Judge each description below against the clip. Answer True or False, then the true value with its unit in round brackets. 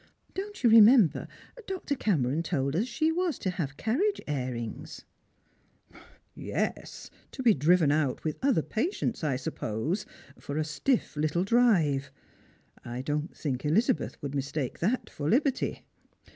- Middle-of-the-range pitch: True (165 Hz)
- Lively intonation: True (8.9 semitones)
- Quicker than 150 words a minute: False (145 wpm)